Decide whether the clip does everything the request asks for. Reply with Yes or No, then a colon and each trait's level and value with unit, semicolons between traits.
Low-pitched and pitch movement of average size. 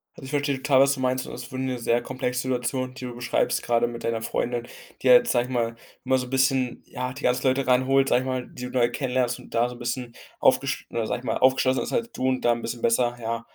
No: low, 125 Hz; narrow, 1.5 semitones